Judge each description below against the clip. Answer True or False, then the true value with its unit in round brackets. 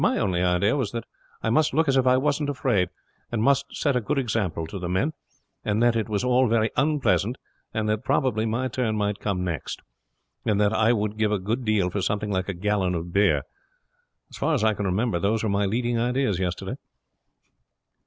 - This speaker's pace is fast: True (215 wpm)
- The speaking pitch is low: True (110 Hz)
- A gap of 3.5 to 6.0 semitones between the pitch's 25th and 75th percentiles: True (3.9 semitones)